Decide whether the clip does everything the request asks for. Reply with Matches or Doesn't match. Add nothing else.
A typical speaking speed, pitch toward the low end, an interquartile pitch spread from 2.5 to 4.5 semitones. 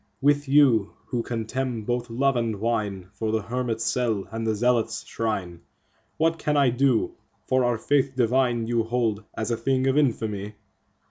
Matches